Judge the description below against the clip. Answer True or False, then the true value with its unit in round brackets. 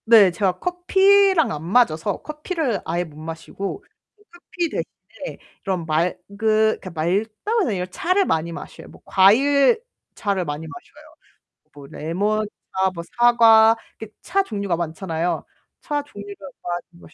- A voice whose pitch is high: True (205 Hz)